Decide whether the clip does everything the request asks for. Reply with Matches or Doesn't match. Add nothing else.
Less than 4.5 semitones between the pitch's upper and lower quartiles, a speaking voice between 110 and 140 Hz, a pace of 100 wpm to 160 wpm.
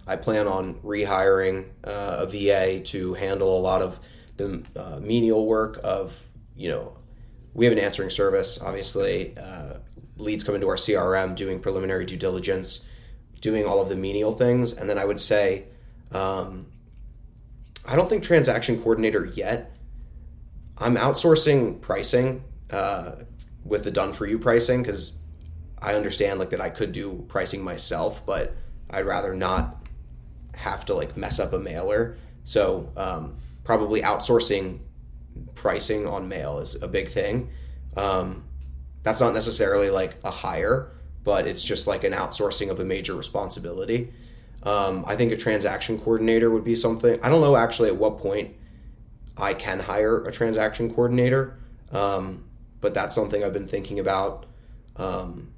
Doesn't match